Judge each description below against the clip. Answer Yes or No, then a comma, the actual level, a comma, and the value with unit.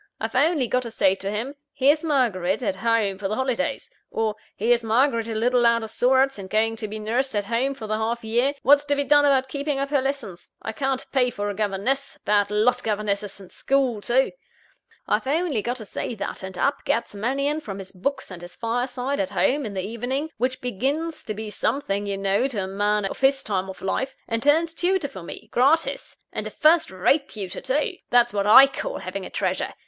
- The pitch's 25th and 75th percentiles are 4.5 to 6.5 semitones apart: Yes, average, 4.8 semitones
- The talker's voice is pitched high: Yes, high, 240 Hz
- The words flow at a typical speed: No, fast, 220 wpm